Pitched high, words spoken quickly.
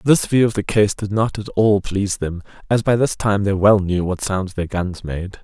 No: low, 100 Hz; fast, 255 wpm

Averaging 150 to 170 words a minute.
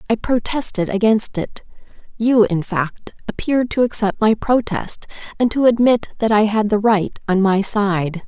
Yes: average, 165 wpm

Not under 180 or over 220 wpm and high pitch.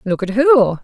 Yes: fast, 215 wpm; high, 230 Hz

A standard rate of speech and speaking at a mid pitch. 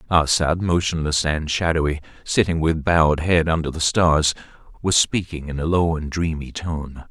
No: average, 160 wpm; very low, 80 Hz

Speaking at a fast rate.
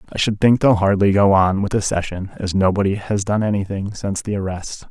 Yes: fast, 220 wpm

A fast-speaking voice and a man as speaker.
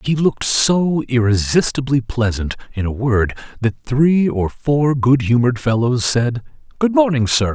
No: average, 150 wpm; male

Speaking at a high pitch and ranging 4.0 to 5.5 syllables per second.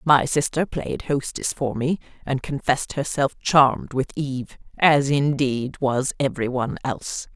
No: low, 135 Hz; 4.7 syllables/s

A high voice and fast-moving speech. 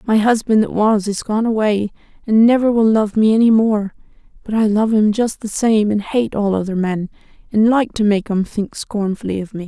Yes: high, 215 Hz; fast, 215 wpm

